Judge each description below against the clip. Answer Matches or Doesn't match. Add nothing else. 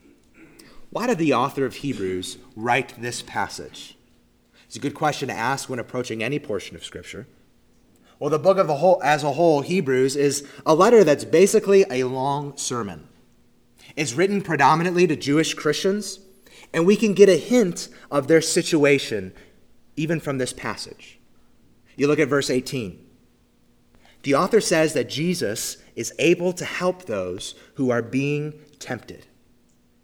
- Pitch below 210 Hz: Matches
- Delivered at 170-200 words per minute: Doesn't match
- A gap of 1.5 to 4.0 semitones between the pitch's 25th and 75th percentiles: Doesn't match